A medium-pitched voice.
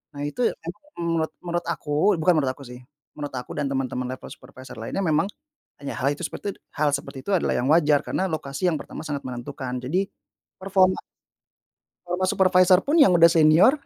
Yes: medium, 155 Hz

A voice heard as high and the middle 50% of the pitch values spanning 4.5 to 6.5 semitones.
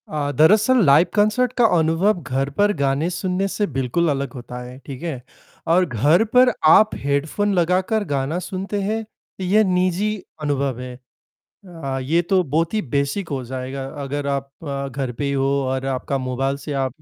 No: medium, 150 Hz; wide, 5.5 semitones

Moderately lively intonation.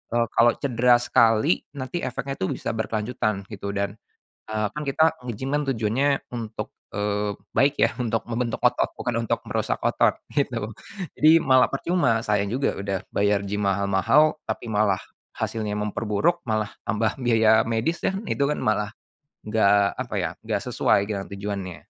Yes: average, 3.9 semitones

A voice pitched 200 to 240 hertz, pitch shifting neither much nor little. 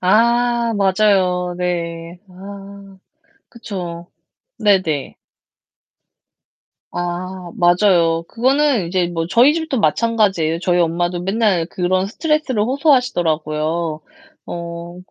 No: medium, 185 Hz; average, 4.2 semitones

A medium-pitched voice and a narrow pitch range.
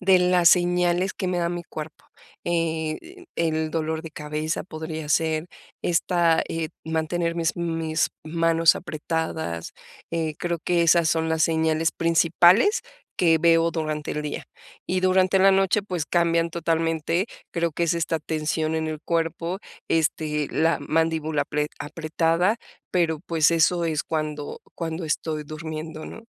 Yes: medium, 165 Hz; narrow, 1.5 semitones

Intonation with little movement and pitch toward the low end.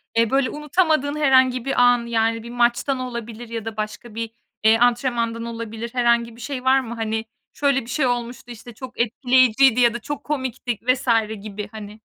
No: narrow, 2.3 semitones; high, 240 Hz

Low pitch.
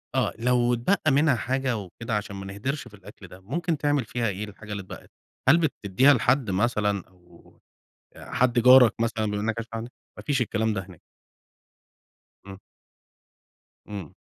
Yes: low, 115 Hz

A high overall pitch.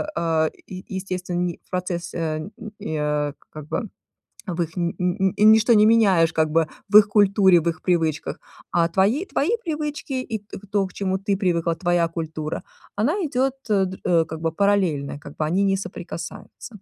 No: medium, 180 Hz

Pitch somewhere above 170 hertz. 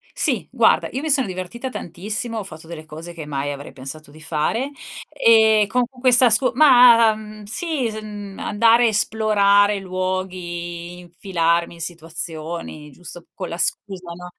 Yes: high, 190 Hz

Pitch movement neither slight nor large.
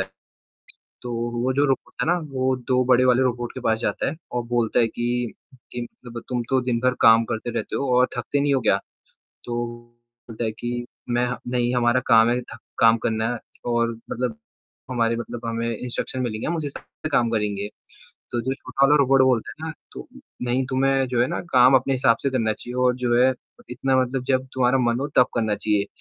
No: narrow, 1.8 semitones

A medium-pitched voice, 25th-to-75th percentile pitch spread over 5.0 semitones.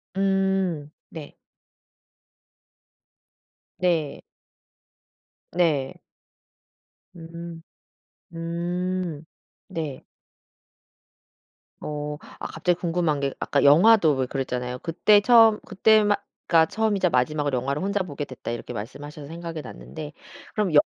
No: medium, 165 Hz; average, 4.1 semitones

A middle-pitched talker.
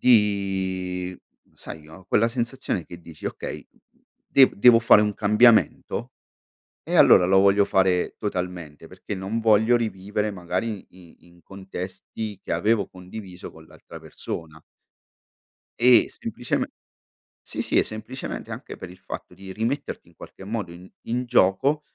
No: very low, 95 Hz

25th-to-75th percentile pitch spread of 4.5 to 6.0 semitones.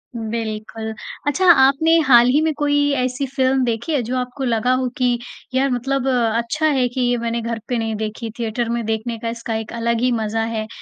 No: narrow, 2.6 semitones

